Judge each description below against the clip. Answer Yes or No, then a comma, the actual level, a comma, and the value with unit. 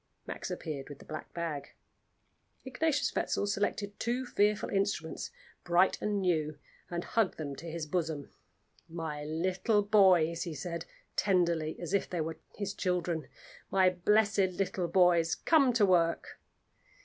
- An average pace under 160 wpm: Yes, average, 140 wpm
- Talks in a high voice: No, medium, 180 Hz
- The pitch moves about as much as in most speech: Yes, average, 3.7 semitones